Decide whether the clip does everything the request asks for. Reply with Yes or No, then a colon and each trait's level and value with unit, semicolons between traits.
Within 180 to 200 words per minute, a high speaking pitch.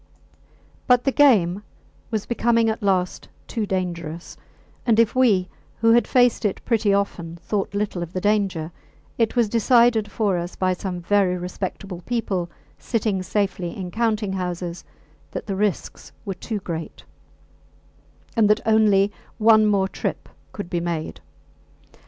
No: average, 145 wpm; high, 200 Hz